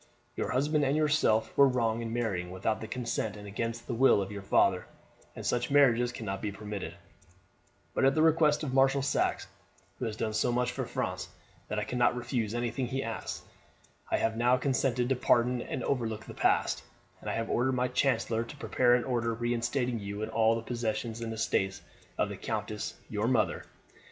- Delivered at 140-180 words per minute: No, average, 190 wpm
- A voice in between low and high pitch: No, low, 120 Hz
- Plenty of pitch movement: No, narrow, 2.4 semitones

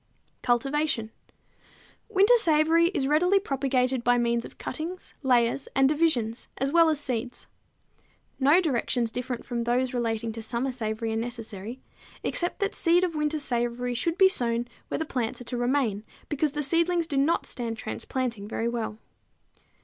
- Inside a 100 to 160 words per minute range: Yes, average, 155 wpm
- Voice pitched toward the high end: Yes, very high, 255 Hz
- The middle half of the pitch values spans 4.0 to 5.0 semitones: Yes, average, 4.7 semitones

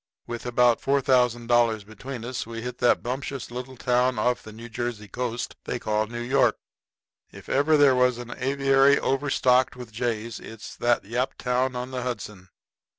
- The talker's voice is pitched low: Yes, low, 125 Hz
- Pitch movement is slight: Yes, narrow, 1.7 semitones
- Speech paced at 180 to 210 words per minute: No, average, 165 wpm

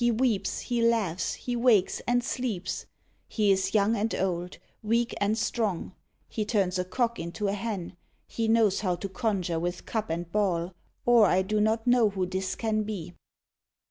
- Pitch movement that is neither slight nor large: Yes, average, 3.7 semitones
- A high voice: Yes, high, 210 Hz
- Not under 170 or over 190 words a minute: Yes, average, 175 wpm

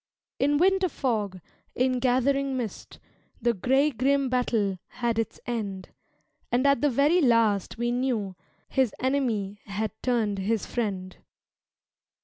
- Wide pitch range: No, average, 4.1 semitones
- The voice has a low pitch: No, high, 240 Hz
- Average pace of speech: No, slow, 130 wpm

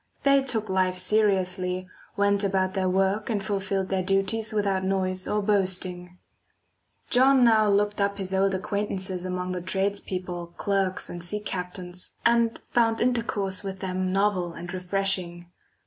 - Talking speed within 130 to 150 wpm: Yes, average, 145 wpm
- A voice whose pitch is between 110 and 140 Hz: No, high, 195 Hz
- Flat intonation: Yes, narrow, 2.0 semitones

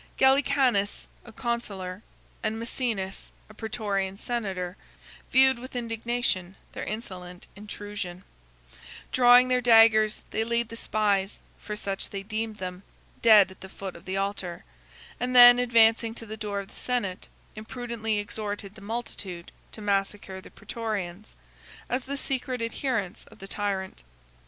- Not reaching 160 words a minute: Yes, average, 140 wpm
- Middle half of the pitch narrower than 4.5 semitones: Yes, average, 3.3 semitones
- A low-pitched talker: No, high, 215 Hz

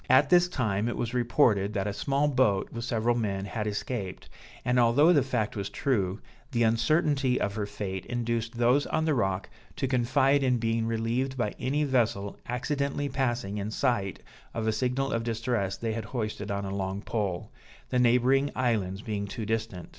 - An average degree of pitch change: Yes, average, 3.9 semitones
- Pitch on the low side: Yes, low, 115 Hz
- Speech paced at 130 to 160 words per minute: No, average, 185 wpm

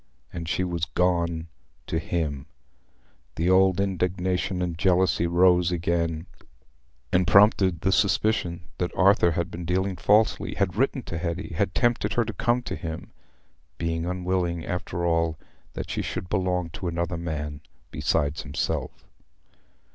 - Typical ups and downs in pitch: No, narrow, 2.0 semitones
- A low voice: Yes, very low, 90 Hz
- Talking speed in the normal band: No, slow, 130 wpm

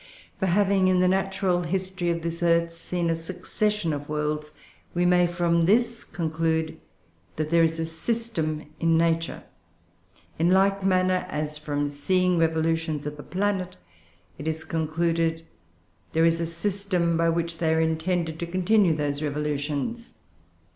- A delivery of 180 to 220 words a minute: No, average, 155 wpm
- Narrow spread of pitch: Yes, narrow, 2.3 semitones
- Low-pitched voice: No, medium, 165 Hz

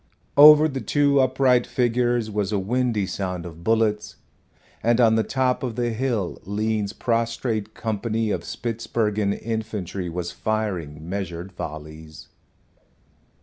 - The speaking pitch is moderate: No, low, 110 Hz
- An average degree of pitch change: Yes, average, 3.8 semitones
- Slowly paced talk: Yes, slow, 125 wpm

